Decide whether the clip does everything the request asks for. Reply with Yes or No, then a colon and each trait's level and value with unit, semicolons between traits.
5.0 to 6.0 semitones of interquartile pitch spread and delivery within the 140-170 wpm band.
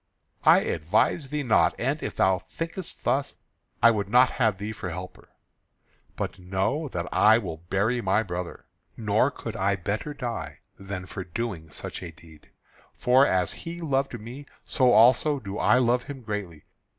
Yes: wide, 5.4 semitones; average, 165 wpm